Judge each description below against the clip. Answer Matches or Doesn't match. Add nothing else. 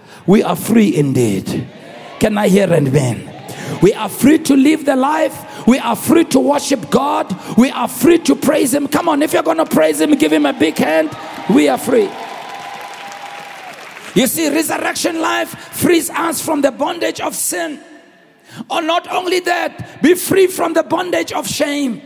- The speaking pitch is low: Doesn't match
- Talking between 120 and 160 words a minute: Doesn't match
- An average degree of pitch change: Doesn't match